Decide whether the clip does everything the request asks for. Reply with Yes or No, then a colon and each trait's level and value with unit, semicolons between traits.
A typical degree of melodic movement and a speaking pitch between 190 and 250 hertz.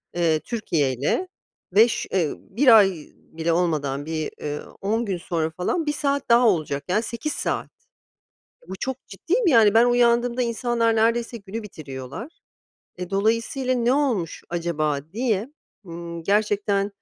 No: wide, 6.1 semitones; high, 205 Hz